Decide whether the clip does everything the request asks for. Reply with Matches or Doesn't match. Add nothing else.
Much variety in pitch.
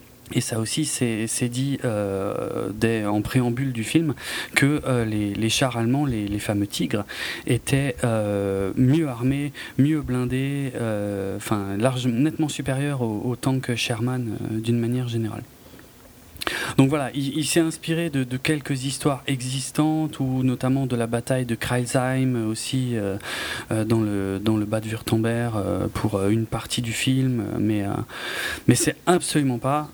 Doesn't match